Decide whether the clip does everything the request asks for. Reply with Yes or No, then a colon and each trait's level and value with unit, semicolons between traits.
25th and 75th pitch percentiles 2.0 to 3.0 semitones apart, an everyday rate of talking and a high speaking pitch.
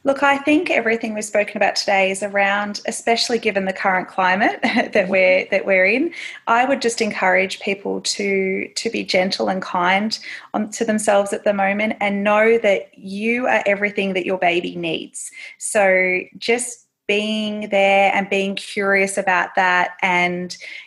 Yes: average, 2.7 semitones; average, 165 wpm; high, 205 Hz